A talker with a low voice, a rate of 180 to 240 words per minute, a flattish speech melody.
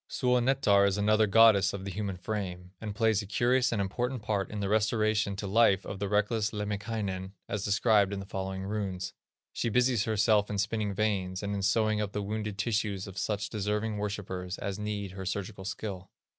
Yes: low, 105 Hz; average, 190 wpm; narrow, 1.9 semitones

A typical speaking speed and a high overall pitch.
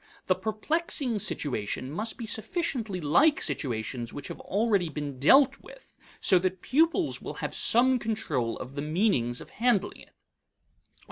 Yes: average, 145 wpm; high, 200 Hz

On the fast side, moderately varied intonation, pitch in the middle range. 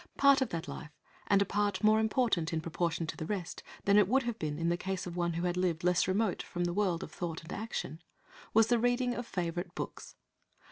Yes: fast, 235 wpm; average, 4.2 semitones; medium, 180 Hz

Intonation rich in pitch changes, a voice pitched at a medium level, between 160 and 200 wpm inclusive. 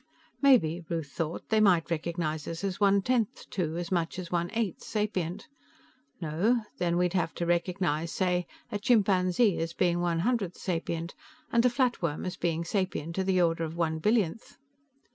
No: average, 3.2 semitones; medium, 175 Hz; average, 175 wpm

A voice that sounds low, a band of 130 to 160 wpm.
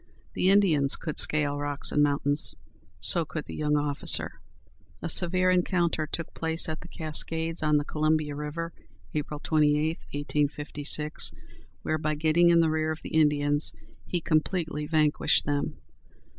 No: medium, 155 Hz; average, 145 wpm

